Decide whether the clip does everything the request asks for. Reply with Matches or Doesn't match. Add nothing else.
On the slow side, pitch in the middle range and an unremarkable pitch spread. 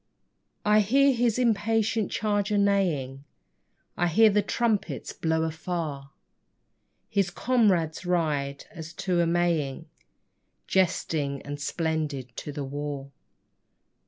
Doesn't match